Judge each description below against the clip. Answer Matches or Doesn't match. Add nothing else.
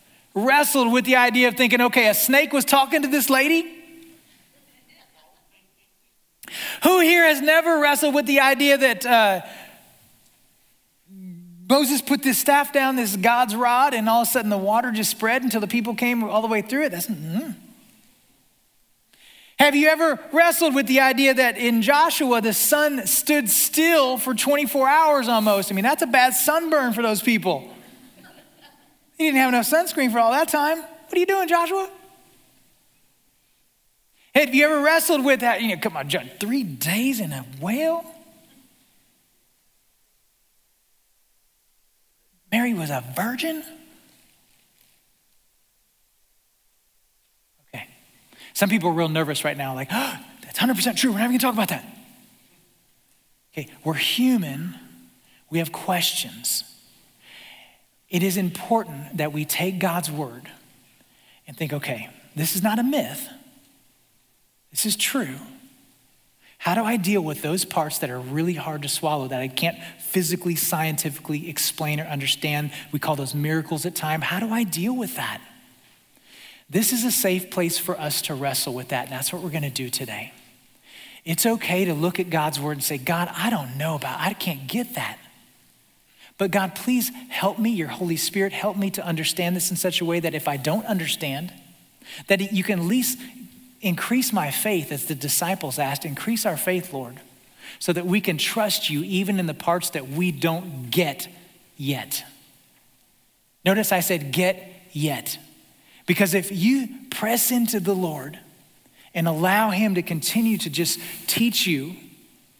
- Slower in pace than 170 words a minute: Matches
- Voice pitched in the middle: Doesn't match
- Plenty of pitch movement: Matches